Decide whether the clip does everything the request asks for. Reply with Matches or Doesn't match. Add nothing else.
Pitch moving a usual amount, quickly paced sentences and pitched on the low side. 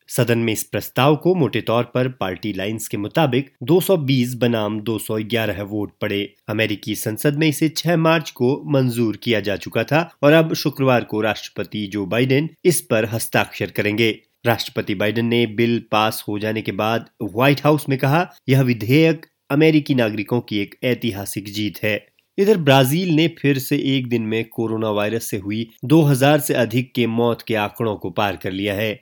Doesn't match